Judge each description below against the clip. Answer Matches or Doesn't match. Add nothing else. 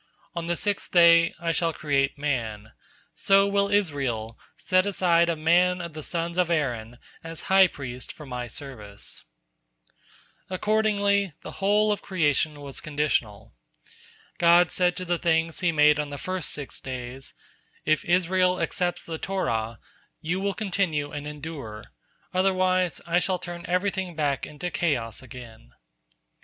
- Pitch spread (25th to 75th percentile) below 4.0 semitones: Doesn't match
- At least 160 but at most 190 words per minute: Doesn't match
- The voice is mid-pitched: Matches